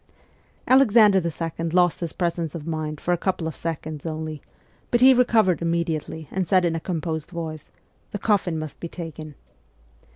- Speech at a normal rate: Yes, average, 170 wpm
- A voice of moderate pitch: Yes, medium, 170 Hz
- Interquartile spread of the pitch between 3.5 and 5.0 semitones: No, average, 2.8 semitones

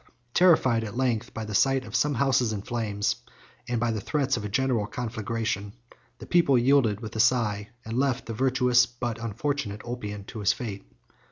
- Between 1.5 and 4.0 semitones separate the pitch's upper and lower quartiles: Yes, average, 3.2 semitones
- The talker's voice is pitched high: No, low, 120 Hz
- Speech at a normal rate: Yes, average, 185 wpm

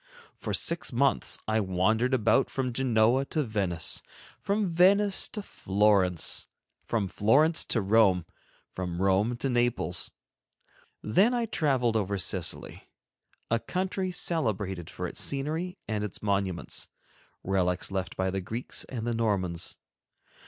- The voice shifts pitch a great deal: Yes, wide, 6.3 semitones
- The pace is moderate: No, slow, 130 wpm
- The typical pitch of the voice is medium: No, low, 110 Hz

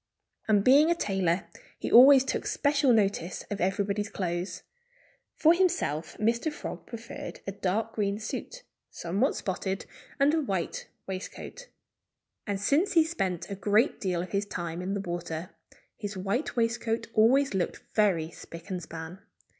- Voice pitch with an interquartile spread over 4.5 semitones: Yes, average, 5.2 semitones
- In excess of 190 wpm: No, average, 150 wpm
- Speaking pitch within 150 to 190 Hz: No, high, 205 Hz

